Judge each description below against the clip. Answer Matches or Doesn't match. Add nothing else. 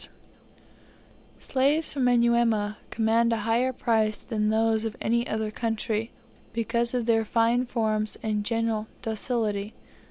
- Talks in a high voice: Matches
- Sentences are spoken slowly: Matches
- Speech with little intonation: Matches